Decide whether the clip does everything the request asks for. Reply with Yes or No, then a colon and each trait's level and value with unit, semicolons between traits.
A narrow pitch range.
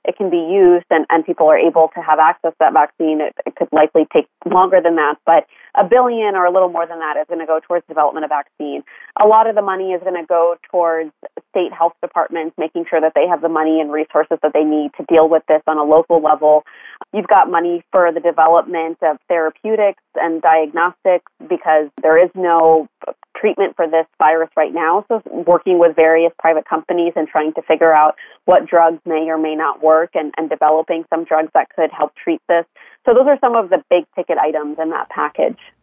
Yes: narrow, 1.9 semitones